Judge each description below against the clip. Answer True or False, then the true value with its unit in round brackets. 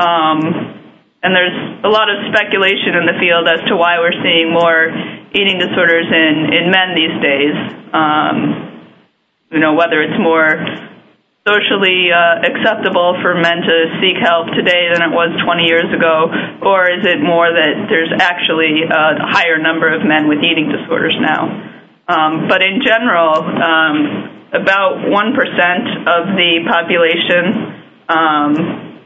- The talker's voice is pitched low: False (170 Hz)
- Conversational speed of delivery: True (145 wpm)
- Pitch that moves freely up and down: False (2.7 semitones)